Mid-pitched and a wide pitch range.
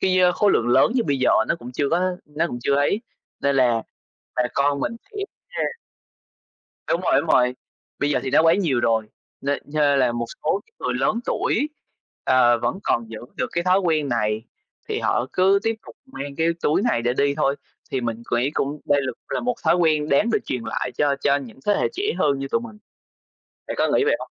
Yes: medium, 145 Hz; wide, 6.1 semitones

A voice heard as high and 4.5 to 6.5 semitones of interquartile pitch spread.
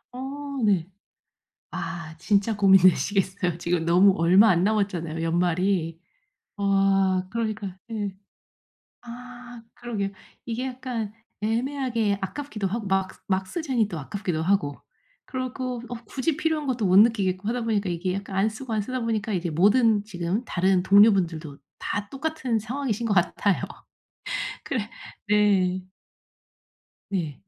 No: high, 200 Hz; average, 3.9 semitones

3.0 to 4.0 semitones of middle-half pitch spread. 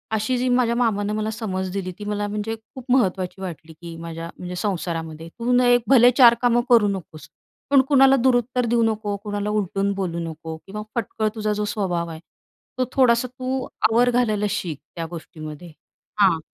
No: average, 5.0 semitones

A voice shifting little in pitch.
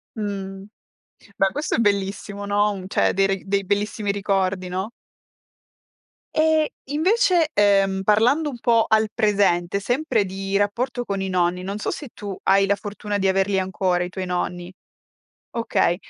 Yes: narrow, 2.3 semitones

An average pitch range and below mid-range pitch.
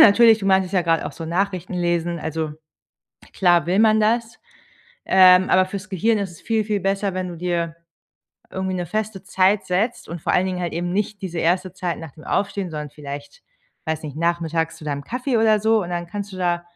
No: average, 3.1 semitones; medium, 185 Hz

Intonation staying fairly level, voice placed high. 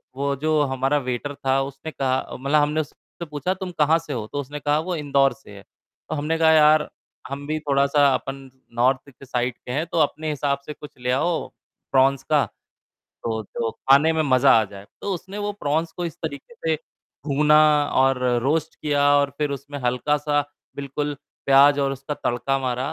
No: narrow, 2.2 semitones; medium, 145 Hz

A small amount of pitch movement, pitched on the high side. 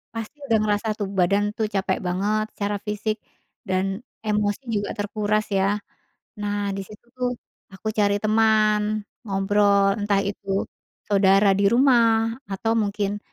Yes: narrow, 1.4 semitones; high, 205 Hz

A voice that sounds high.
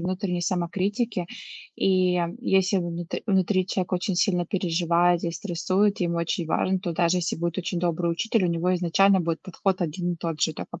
No: medium, 180 Hz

